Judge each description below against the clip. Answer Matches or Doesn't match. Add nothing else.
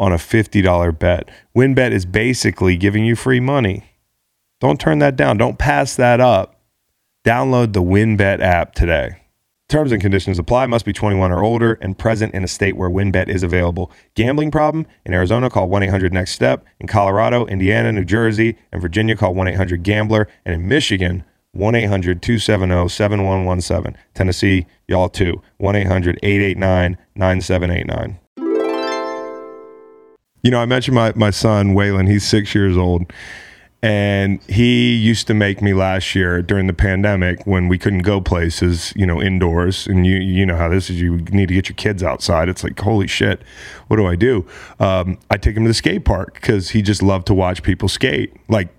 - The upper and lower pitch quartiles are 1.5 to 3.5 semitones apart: Matches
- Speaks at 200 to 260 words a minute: Doesn't match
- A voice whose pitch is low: Matches